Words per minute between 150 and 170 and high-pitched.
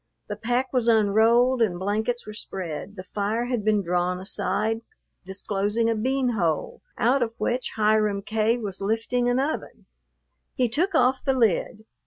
Yes: average, 160 wpm; high, 220 Hz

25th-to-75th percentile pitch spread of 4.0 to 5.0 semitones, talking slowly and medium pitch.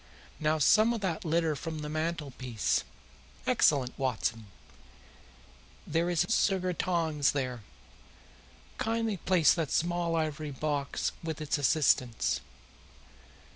No: average, 3.3 semitones; slow, 110 wpm; medium, 155 Hz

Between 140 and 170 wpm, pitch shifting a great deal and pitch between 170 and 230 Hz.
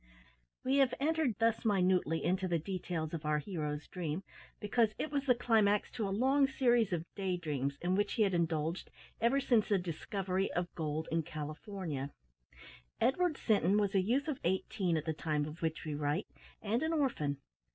No: average, 185 wpm; wide, 6.3 semitones; high, 190 Hz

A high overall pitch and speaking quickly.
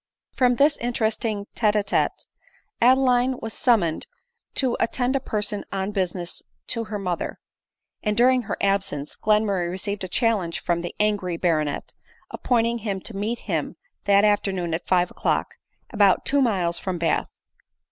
No: high, 205 Hz; average, 155 wpm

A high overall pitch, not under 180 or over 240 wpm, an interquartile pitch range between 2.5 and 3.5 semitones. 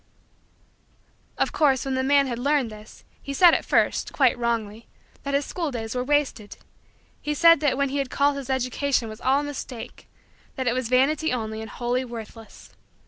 Yes: very high, 260 Hz; average, 190 wpm; average, 3.1 semitones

